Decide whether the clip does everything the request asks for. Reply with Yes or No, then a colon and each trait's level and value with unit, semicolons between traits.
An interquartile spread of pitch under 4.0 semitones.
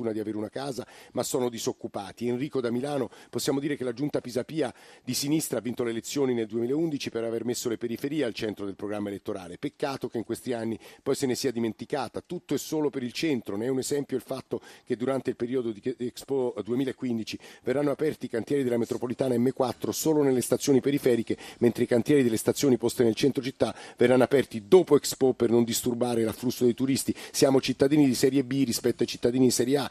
Yes: average, 2.8 semitones